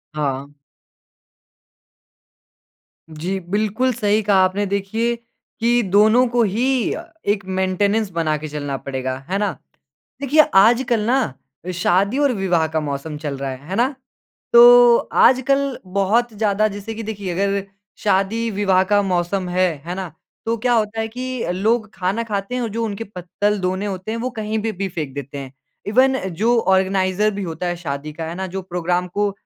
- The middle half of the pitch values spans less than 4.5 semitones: Yes, average, 4.0 semitones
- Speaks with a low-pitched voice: No, high, 200 Hz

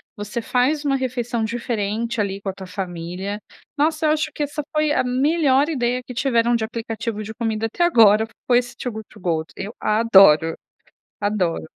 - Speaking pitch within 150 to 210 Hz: No, high, 230 Hz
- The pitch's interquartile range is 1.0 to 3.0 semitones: No, average, 4.0 semitones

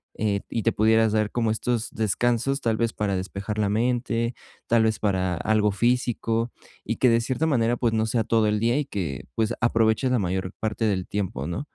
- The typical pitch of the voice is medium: No, low, 110 Hz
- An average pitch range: No, narrow, 2.2 semitones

